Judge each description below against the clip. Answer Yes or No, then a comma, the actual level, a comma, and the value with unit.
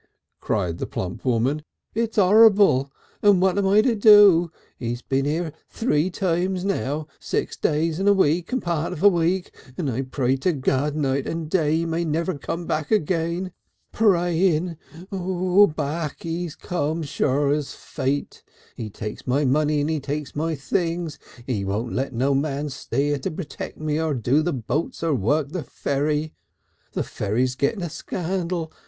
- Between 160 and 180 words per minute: Yes, average, 170 wpm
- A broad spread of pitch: No, average, 4.2 semitones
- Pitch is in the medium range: Yes, medium, 155 Hz